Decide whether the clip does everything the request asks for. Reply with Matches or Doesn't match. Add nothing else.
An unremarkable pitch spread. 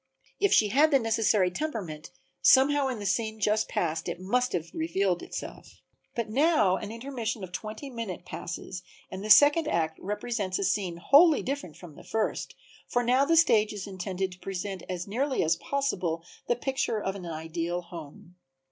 Doesn't match